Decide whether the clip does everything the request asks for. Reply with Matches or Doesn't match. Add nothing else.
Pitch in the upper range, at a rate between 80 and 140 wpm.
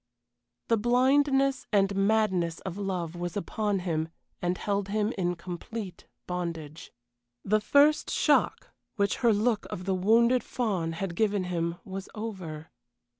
Matches